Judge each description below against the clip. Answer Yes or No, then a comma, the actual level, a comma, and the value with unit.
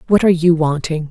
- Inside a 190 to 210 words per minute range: No, fast, 220 wpm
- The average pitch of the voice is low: No, medium, 165 Hz